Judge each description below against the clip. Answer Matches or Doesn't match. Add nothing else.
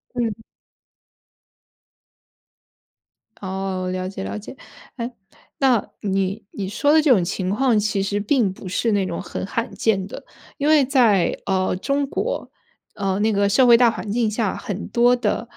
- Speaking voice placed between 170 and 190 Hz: Doesn't match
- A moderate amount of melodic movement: Matches